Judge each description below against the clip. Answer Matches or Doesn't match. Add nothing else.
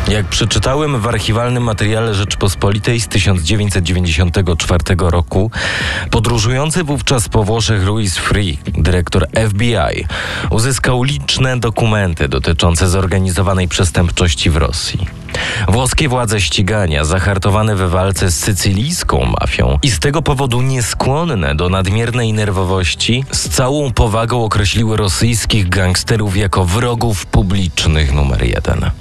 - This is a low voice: Matches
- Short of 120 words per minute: Matches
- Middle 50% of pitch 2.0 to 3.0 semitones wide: Doesn't match